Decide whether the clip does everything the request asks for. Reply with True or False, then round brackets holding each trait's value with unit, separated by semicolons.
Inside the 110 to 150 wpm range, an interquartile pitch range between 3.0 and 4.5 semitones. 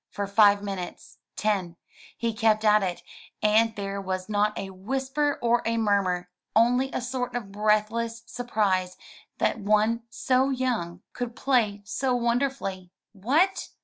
True (140 wpm; 3.5 semitones)